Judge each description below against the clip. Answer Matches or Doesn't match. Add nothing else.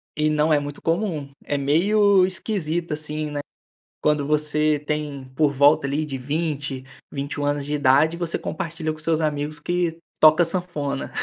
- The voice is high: Doesn't match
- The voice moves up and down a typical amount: Doesn't match